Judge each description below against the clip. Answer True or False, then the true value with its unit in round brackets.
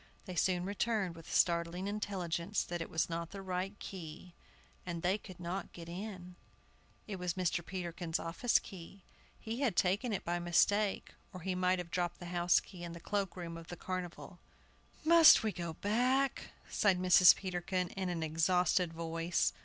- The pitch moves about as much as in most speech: False (2.3 semitones)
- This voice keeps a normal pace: True (175 wpm)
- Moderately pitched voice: True (180 Hz)